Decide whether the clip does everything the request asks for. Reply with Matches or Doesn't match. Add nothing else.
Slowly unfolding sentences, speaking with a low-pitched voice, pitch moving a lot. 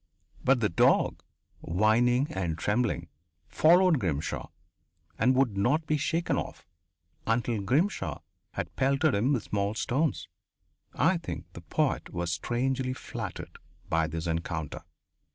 Matches